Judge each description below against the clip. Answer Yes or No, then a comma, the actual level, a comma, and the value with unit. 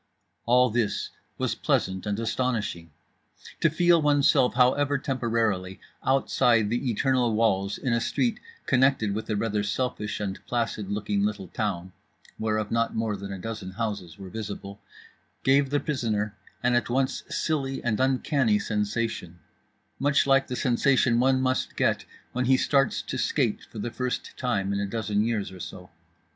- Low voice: Yes, low, 115 Hz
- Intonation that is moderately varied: Yes, average, 4.0 semitones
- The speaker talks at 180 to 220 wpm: No, average, 155 wpm